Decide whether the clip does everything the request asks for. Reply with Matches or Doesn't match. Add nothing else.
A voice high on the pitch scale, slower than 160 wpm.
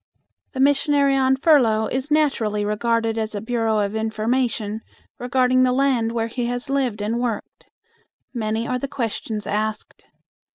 Matches